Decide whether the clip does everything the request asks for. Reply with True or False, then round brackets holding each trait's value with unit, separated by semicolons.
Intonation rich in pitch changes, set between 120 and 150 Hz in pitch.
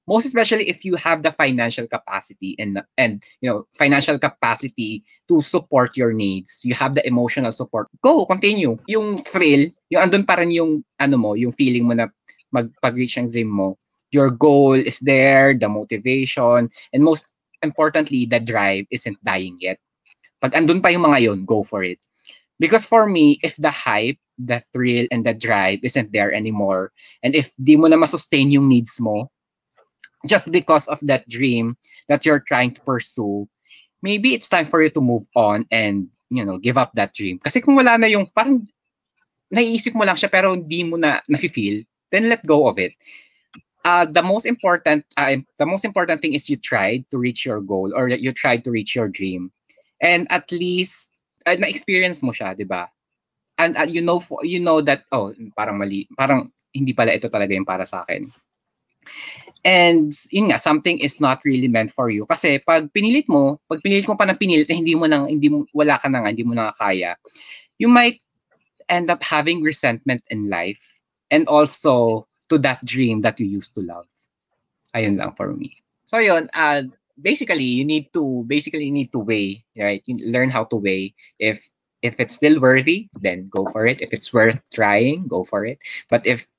True (6.7 semitones; 135 Hz)